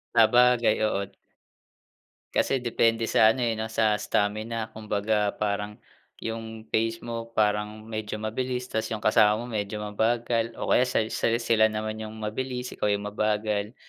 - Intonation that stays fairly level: Yes, narrow, 1.5 semitones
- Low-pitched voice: Yes, low, 110 Hz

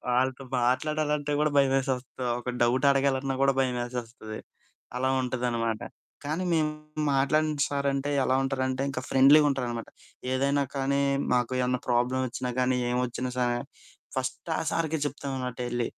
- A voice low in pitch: Yes, low, 130 Hz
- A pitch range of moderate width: No, narrow, 2.0 semitones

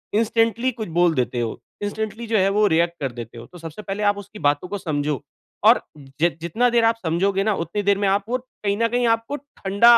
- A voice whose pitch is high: Yes, high, 200 Hz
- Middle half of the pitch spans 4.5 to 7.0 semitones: Yes, average, 5.2 semitones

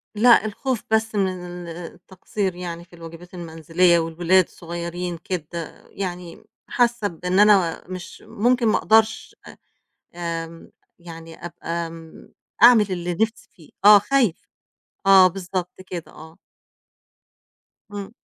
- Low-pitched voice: No, medium, 180 Hz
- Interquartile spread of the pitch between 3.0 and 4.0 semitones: Yes, average, 3.4 semitones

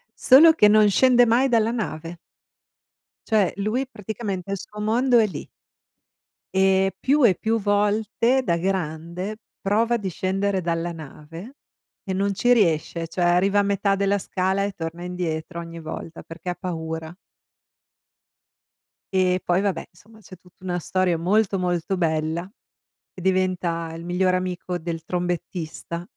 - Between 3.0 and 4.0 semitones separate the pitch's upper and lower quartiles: Yes, average, 3.4 semitones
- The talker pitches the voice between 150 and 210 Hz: Yes, medium, 185 Hz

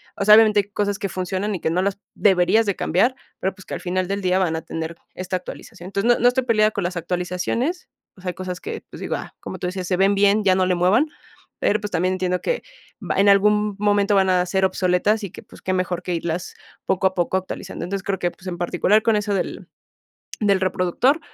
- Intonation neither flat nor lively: No, narrow, 2.3 semitones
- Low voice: No, high, 190 Hz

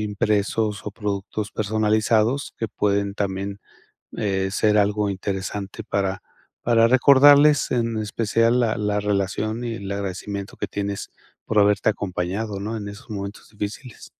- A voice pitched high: No, low, 105 Hz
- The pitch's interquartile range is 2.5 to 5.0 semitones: No, narrow, 1.8 semitones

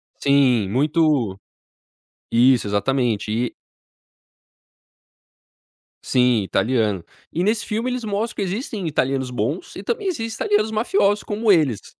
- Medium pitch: Yes, medium, 145 Hz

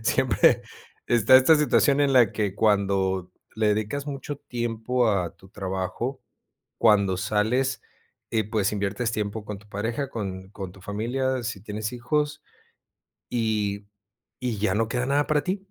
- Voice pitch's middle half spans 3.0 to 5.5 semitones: Yes, average, 3.9 semitones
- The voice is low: Yes, low, 110 Hz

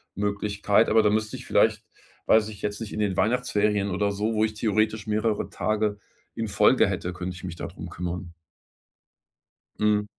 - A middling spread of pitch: No, narrow, 1.4 semitones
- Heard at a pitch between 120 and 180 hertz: No, low, 105 Hz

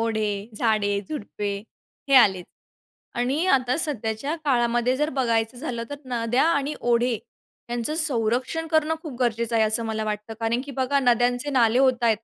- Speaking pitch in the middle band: No, high, 240 Hz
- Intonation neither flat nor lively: Yes, average, 3.3 semitones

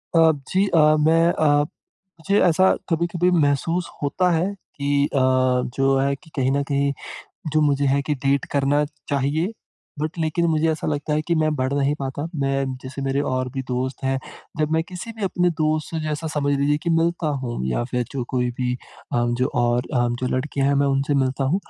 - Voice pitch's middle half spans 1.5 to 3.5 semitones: Yes, average, 3.1 semitones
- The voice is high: No, medium, 145 Hz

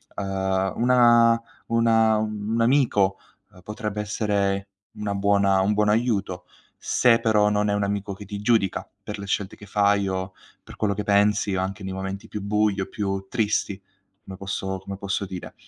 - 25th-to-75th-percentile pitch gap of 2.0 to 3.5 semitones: No, narrow, 1.6 semitones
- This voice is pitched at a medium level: No, low, 100 Hz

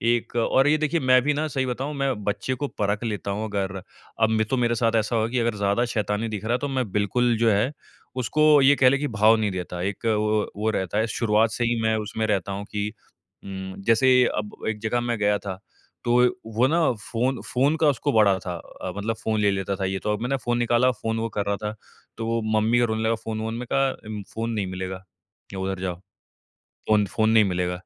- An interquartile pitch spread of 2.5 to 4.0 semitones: Yes, average, 2.9 semitones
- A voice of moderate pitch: No, low, 110 Hz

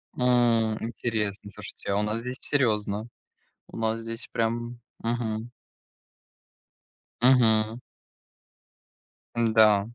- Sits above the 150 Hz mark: No, low, 115 Hz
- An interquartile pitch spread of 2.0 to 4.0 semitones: No, narrow, 1.6 semitones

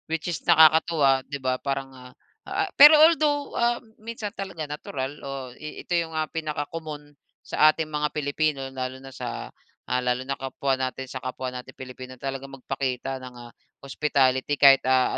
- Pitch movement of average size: Yes, average, 3.4 semitones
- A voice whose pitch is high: No, medium, 140 Hz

